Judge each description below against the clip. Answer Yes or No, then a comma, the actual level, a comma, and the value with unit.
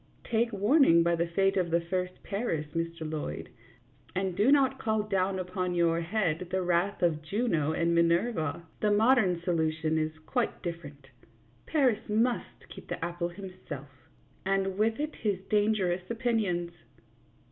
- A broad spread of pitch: No, average, 4.1 semitones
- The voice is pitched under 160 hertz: No, medium, 185 Hz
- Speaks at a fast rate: No, average, 145 wpm